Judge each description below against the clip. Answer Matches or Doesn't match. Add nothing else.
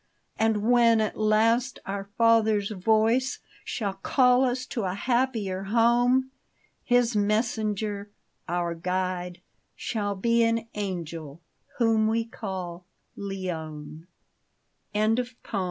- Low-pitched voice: Doesn't match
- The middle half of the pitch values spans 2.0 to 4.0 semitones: Matches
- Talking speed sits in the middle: Doesn't match